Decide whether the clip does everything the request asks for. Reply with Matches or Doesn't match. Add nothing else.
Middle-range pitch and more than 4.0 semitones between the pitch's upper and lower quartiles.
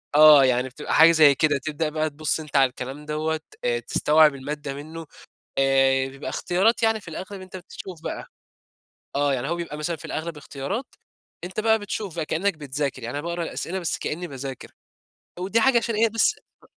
Matches